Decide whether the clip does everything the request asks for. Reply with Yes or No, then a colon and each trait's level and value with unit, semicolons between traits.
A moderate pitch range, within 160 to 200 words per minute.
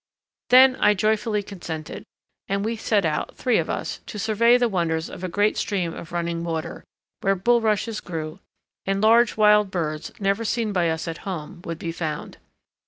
Yes: average, 4.6 semitones; average, 175 wpm